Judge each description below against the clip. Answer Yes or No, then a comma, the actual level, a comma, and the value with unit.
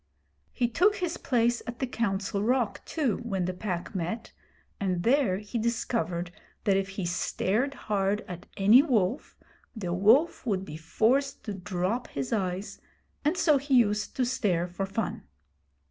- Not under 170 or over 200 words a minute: No, average, 160 wpm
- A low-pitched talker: No, high, 210 Hz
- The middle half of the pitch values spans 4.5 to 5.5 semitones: Yes, average, 4.8 semitones